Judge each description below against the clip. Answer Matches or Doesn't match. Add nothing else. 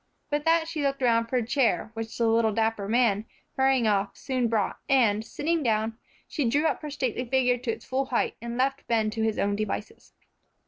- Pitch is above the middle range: Matches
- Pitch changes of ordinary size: Matches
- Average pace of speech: Doesn't match